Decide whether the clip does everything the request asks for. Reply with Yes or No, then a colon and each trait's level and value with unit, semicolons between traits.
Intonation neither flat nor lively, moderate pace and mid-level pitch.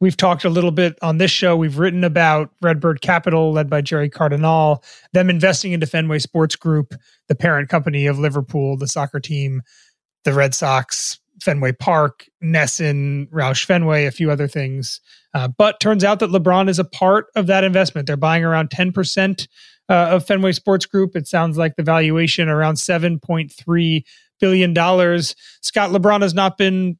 Yes: average, 3.5 semitones; average, 170 wpm; medium, 165 Hz